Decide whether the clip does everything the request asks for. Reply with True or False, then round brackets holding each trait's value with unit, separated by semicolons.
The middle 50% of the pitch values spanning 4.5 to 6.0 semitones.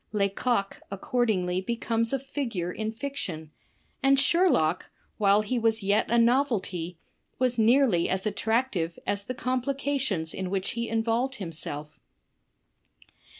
True (5.1 semitones)